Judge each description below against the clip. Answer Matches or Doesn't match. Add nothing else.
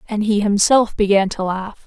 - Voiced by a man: Doesn't match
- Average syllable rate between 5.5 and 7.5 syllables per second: Doesn't match